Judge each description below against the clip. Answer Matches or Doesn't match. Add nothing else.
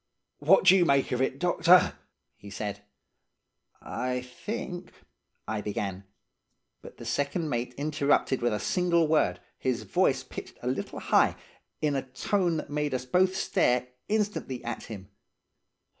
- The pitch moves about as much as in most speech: Doesn't match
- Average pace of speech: Matches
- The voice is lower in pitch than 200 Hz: Matches